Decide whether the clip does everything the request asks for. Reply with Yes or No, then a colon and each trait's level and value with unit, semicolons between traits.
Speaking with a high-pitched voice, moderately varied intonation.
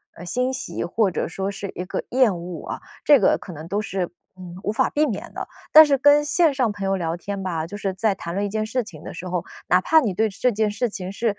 Yes: high, 200 Hz; average, 5.0 semitones